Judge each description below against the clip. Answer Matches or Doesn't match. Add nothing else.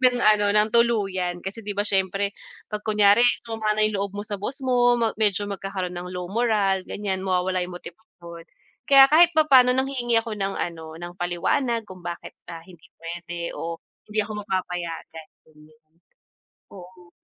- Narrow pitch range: Doesn't match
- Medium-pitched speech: Doesn't match